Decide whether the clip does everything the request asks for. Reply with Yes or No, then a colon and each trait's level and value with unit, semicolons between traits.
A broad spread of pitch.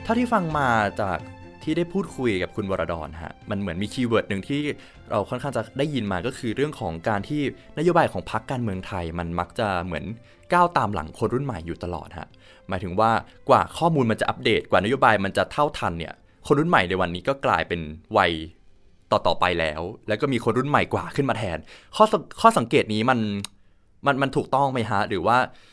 Yes: wide, 6.9 semitones